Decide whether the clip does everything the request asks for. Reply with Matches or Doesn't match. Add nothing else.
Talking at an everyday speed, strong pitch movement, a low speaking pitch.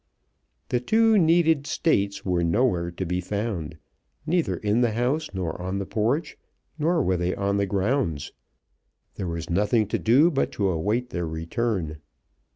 Matches